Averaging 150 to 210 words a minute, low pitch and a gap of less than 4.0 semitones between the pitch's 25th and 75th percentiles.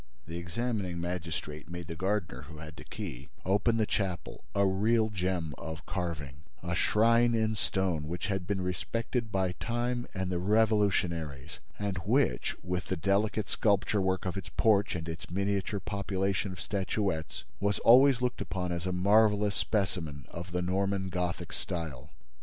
Yes: average, 160 wpm; very low, 95 Hz; average, 3.4 semitones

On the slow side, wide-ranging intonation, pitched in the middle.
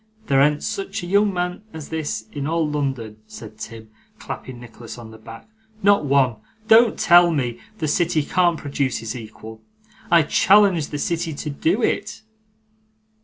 No: average, 165 wpm; wide, 6.4 semitones; medium, 150 Hz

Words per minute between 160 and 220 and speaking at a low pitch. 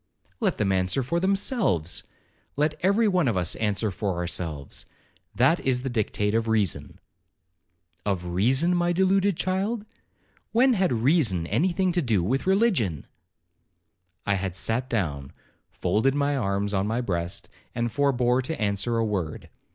No: average, 140 wpm; low, 120 Hz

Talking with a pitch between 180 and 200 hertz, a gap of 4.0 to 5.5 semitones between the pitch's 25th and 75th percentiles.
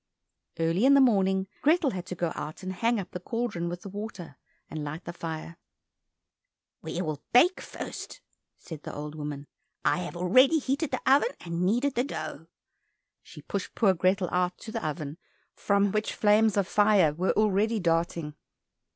Yes: medium, 185 Hz; average, 4.7 semitones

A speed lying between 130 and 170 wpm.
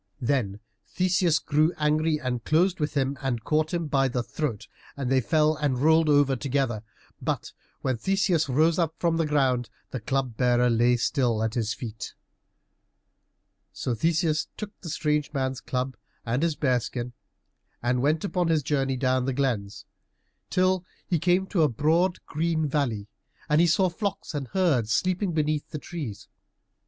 Yes: average, 165 wpm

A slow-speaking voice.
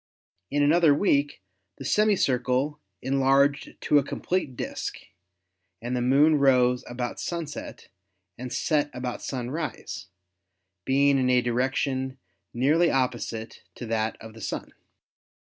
Yes: slow, 130 wpm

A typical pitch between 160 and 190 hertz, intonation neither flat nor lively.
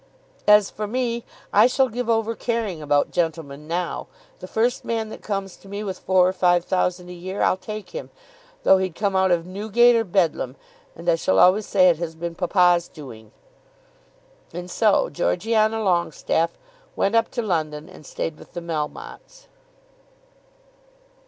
Yes: medium, 185 Hz; average, 4.1 semitones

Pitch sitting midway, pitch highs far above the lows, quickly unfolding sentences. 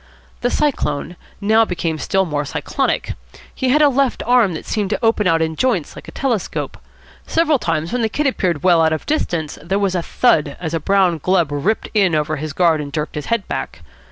Yes: medium, 180 Hz; wide, 6.2 semitones; fast, 215 wpm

